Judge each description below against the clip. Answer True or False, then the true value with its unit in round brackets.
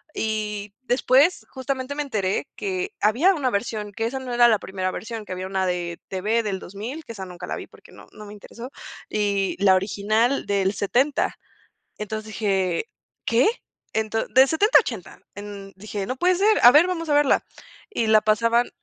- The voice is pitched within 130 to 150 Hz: False (220 Hz)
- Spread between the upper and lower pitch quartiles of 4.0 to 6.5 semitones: True (4.6 semitones)